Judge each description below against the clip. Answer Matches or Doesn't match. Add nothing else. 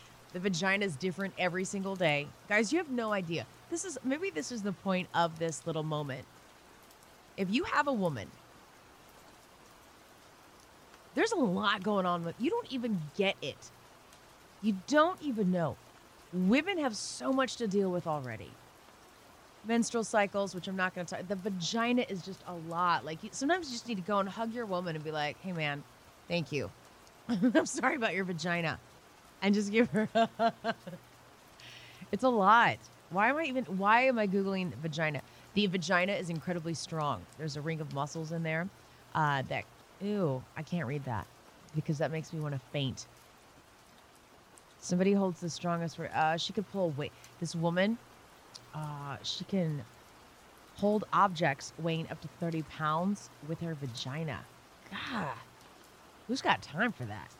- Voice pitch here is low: Doesn't match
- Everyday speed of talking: Matches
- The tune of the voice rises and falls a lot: Doesn't match